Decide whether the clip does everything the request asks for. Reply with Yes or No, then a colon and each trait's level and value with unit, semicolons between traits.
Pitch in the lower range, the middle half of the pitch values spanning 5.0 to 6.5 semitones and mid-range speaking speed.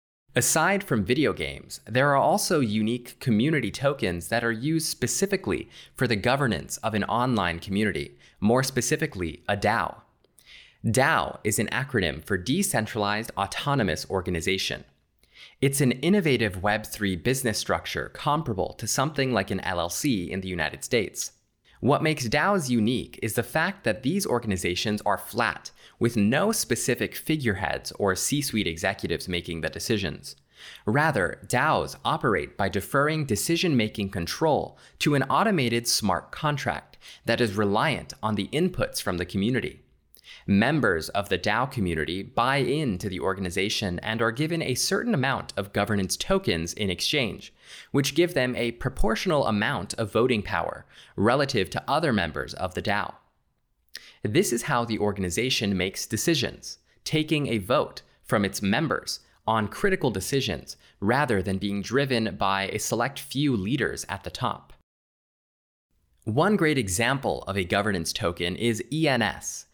Yes: low, 110 Hz; wide, 5.6 semitones; average, 145 wpm